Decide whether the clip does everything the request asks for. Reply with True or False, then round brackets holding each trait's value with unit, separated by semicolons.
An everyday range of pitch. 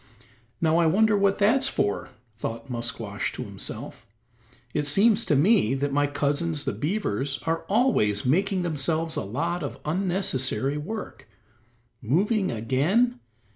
False (6.8 semitones)